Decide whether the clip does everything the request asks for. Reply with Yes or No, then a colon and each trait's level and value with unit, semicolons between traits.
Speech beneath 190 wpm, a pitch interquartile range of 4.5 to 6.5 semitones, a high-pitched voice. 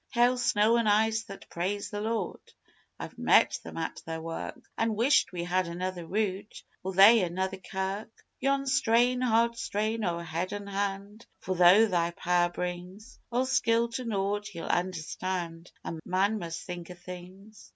No: average, 165 wpm; average, 3.9 semitones; high, 195 Hz